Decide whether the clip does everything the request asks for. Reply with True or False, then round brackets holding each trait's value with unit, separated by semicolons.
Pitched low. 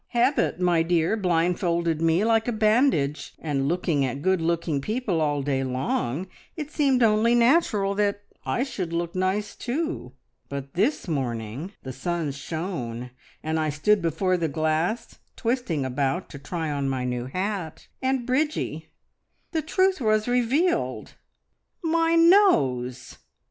False (175 Hz)